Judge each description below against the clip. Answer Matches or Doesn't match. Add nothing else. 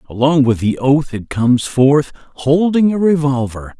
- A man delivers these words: Matches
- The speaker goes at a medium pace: Matches